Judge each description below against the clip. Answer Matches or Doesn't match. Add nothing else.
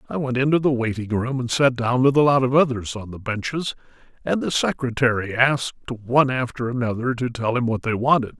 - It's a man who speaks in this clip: Matches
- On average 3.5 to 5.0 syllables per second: Doesn't match